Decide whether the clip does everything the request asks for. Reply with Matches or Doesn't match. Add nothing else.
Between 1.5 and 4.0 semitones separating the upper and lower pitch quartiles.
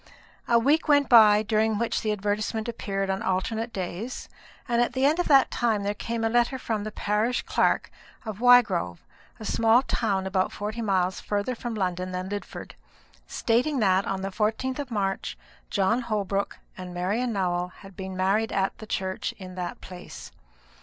Matches